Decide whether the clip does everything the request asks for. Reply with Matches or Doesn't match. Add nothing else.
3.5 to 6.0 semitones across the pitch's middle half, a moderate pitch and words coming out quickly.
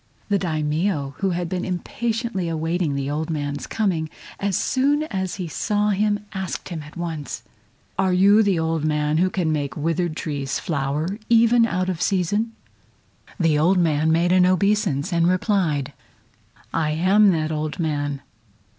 Doesn't match